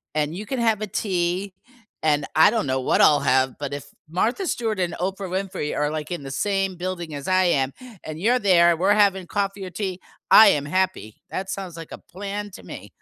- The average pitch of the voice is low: No, medium, 185 Hz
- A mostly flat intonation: No, average, 4.5 semitones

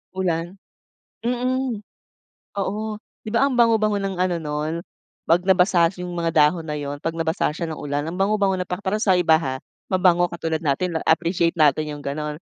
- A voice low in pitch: No, medium, 175 Hz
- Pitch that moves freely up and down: No, average, 3.6 semitones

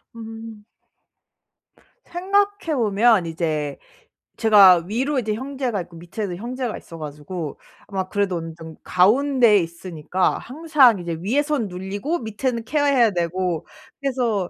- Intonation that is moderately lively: No, wide, 6.3 semitones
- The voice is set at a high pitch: Yes, high, 210 Hz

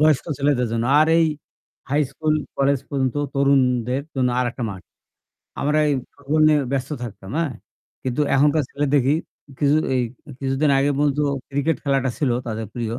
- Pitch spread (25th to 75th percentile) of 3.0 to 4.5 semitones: No, narrow, 2.6 semitones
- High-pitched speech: No, medium, 140 Hz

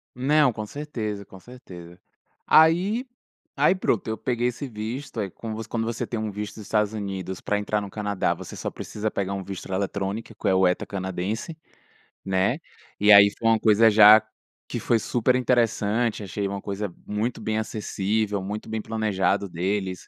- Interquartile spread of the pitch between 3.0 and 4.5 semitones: No, narrow, 2.6 semitones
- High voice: No, low, 105 Hz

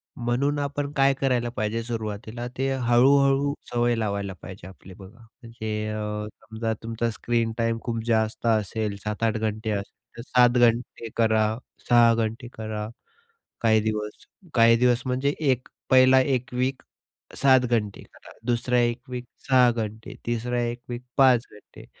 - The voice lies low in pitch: Yes, low, 115 Hz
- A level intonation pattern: Yes, narrow, 2.3 semitones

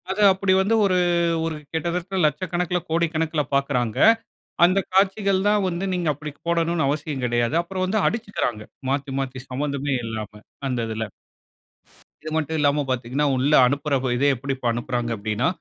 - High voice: No, medium, 150 Hz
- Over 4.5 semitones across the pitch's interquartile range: Yes, wide, 5.6 semitones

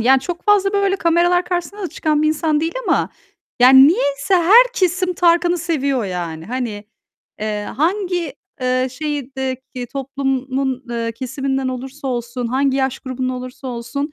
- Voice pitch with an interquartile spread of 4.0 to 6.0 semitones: Yes, average, 5.0 semitones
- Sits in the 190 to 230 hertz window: No, very high, 275 Hz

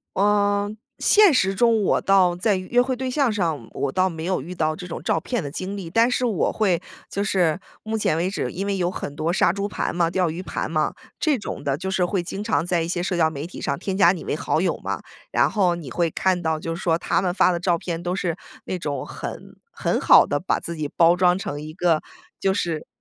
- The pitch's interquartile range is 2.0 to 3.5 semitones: Yes, average, 3.1 semitones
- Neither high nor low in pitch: Yes, medium, 180 Hz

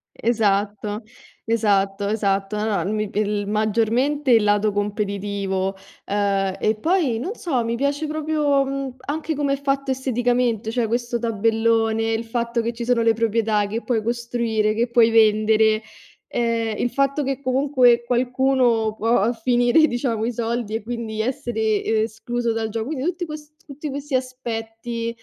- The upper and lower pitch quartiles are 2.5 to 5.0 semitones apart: Yes, average, 2.8 semitones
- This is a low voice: No, high, 230 Hz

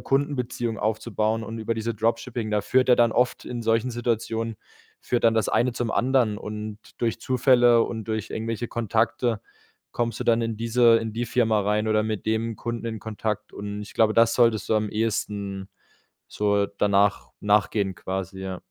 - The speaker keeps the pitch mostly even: Yes, narrow, 1.7 semitones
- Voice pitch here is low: Yes, low, 110 Hz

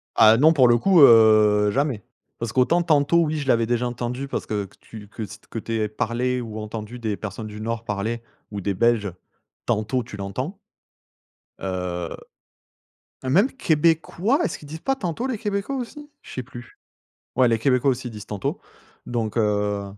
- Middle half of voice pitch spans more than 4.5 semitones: Yes, average, 5.2 semitones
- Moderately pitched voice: No, low, 120 Hz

